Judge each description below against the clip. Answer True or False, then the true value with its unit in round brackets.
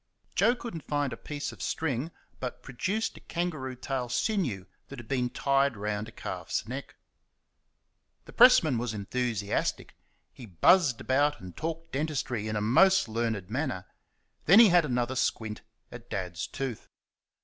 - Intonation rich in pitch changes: True (5.7 semitones)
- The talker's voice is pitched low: True (130 Hz)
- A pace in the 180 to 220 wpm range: False (155 wpm)